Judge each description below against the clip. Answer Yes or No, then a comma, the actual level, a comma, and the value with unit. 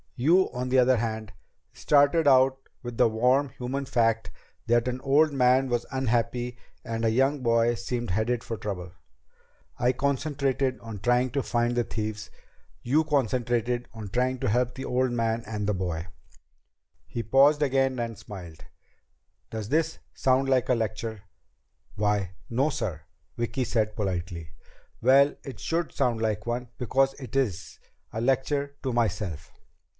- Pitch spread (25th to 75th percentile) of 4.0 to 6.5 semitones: No, average, 3.1 semitones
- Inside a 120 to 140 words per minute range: No, average, 150 wpm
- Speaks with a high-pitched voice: No, low, 120 Hz